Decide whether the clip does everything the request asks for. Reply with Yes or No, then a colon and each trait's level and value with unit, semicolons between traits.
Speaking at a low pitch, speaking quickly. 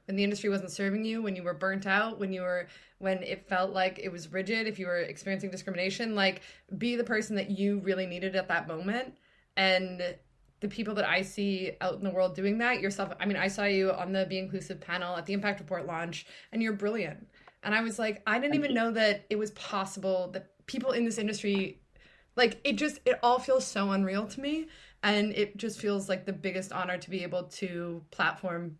No: high, 195 Hz; fast, 225 wpm